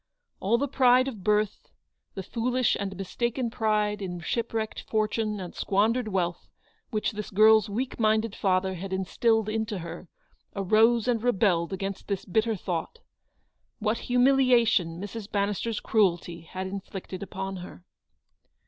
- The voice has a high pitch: Yes, high, 210 Hz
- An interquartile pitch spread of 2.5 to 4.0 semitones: Yes, average, 3.2 semitones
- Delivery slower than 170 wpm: Yes, average, 140 wpm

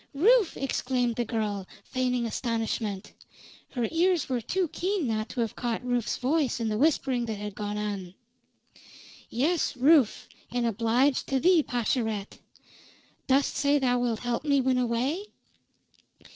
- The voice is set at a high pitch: Yes, high, 245 Hz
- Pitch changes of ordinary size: Yes, average, 3.8 semitones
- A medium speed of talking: Yes, average, 145 wpm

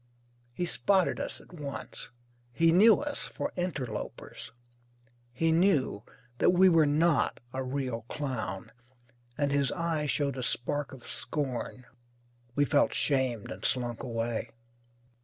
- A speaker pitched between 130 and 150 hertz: Yes, medium, 140 Hz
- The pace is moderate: No, slow, 130 wpm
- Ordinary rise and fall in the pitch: Yes, average, 4.7 semitones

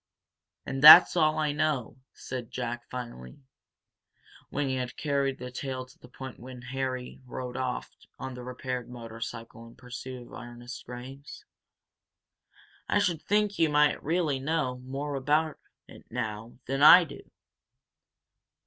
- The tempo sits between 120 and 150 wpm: Yes, average, 140 wpm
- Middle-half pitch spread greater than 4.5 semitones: No, average, 2.9 semitones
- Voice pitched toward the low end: Yes, low, 130 Hz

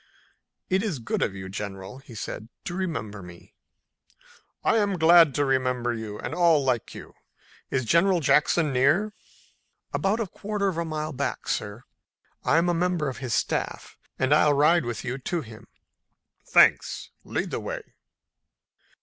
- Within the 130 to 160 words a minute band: Yes, average, 155 wpm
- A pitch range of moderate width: No, wide, 6.5 semitones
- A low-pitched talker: No, medium, 145 Hz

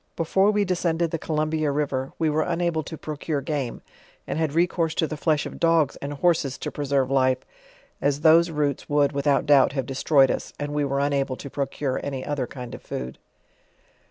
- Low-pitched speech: No, medium, 145 Hz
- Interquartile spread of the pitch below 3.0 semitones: Yes, narrow, 2.6 semitones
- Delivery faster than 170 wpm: Yes, average, 190 wpm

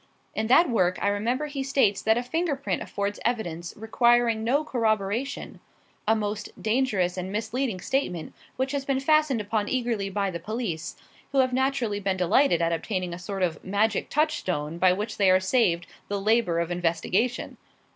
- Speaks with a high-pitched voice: Yes, high, 215 Hz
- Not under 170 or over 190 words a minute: Yes, average, 175 wpm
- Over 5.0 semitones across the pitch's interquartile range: Yes, wide, 5.4 semitones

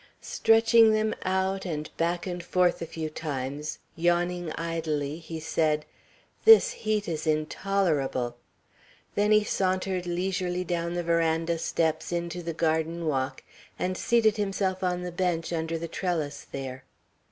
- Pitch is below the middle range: No, medium, 170 Hz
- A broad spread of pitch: No, average, 2.9 semitones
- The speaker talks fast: No, average, 140 wpm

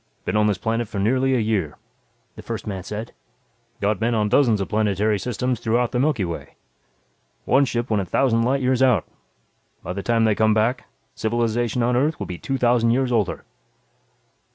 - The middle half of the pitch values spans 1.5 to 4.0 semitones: Yes, average, 2.8 semitones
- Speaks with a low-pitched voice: Yes, low, 115 Hz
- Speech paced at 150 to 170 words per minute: No, average, 190 wpm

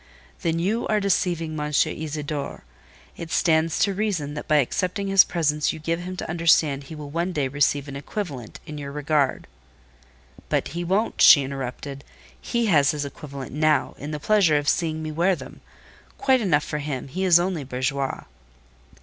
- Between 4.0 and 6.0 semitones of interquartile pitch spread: No, average, 3.6 semitones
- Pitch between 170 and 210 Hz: No, medium, 155 Hz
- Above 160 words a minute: Yes, average, 175 wpm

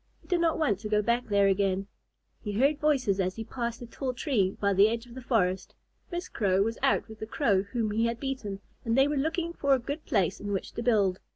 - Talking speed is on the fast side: Yes, fast, 250 wpm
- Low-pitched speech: No, high, 230 Hz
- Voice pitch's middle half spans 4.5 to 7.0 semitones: Yes, average, 5.1 semitones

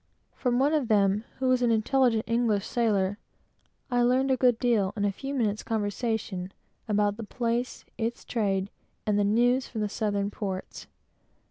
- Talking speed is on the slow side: No, average, 165 wpm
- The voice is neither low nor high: No, high, 225 Hz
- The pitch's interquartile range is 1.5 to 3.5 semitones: Yes, average, 3.1 semitones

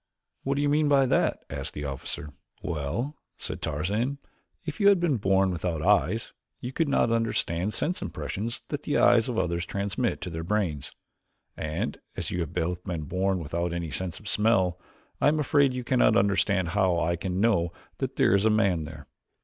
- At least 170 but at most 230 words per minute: Yes, average, 190 wpm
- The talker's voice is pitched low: Yes, very low, 95 Hz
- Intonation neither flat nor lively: No, wide, 5.7 semitones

